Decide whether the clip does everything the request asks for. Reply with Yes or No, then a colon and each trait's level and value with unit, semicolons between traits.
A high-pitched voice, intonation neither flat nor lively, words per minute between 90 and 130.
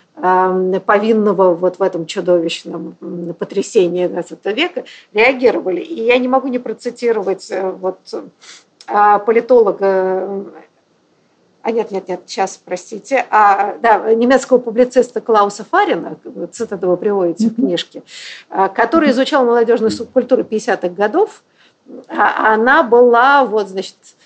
Yes: high, 210 Hz; average, 4.4 semitones; slow, 110 wpm